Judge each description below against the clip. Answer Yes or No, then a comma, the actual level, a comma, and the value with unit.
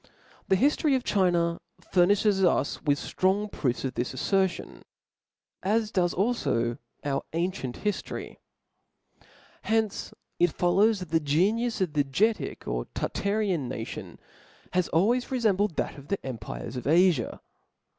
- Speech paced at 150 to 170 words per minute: No, slow, 135 wpm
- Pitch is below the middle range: No, medium, 185 Hz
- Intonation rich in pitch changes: Yes, wide, 6.0 semitones